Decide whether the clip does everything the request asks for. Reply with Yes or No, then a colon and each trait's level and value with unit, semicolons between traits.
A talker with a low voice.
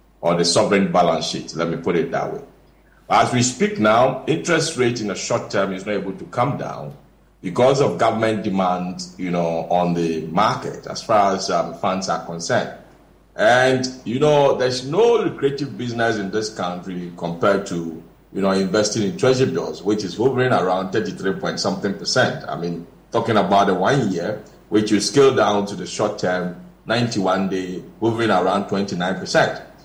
Yes: low, 100 Hz